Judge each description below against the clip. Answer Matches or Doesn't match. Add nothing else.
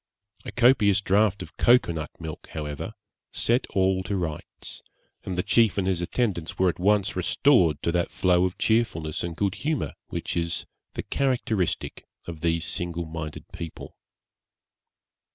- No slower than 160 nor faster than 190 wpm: Doesn't match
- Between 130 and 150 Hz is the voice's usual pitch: Doesn't match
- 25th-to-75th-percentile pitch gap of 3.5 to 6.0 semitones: Matches